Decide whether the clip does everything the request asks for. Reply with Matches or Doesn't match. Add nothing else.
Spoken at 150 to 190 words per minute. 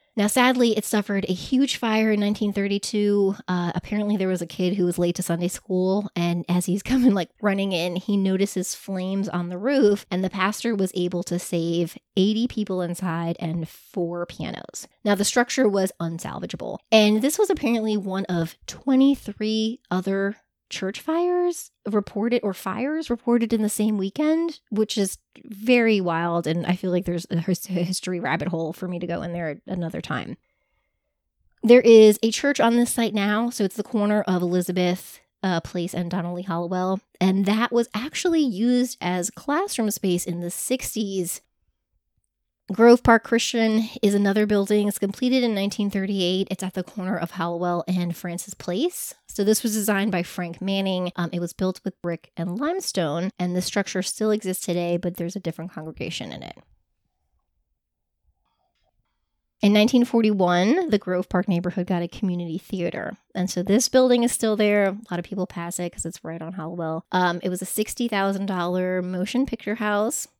Matches